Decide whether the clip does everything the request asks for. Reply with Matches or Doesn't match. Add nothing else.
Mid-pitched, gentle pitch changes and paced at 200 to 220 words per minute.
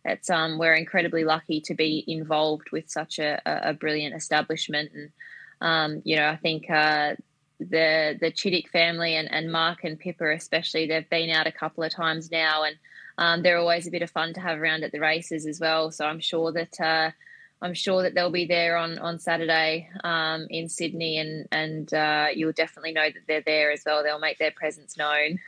Matches